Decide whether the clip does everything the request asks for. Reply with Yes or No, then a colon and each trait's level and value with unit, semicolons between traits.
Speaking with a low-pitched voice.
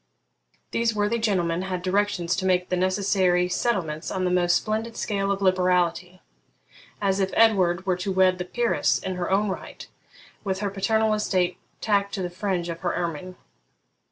No: medium, 185 Hz